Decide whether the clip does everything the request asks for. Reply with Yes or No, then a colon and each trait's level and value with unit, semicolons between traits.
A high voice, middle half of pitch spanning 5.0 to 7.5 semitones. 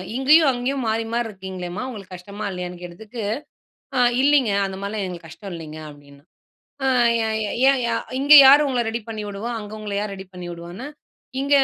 Yes: high, 205 Hz; average, 5.3 semitones